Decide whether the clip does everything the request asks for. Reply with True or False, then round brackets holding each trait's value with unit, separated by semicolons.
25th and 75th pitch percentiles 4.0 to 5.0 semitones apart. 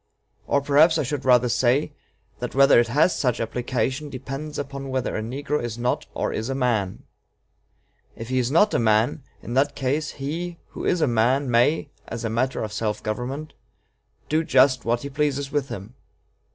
False (3.4 semitones)